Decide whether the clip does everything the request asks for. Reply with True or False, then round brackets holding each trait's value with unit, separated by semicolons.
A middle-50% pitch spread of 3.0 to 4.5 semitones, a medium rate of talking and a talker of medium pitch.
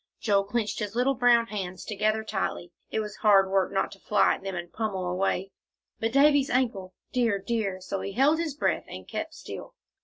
False (3.7 semitones; 195 wpm; 210 Hz)